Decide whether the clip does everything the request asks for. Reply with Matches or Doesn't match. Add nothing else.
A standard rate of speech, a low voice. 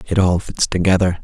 Matches